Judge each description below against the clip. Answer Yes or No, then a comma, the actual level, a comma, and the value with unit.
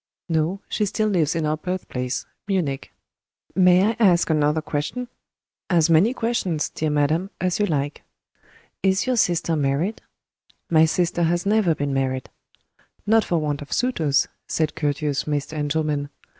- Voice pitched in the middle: Yes, medium, 160 Hz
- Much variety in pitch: No, average, 4.2 semitones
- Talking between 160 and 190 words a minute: No, average, 145 wpm